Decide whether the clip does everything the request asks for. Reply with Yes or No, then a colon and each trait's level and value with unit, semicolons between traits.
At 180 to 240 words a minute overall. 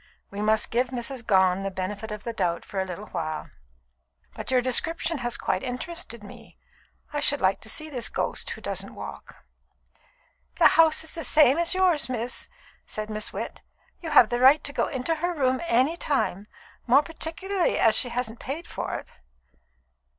Yes: average, 185 wpm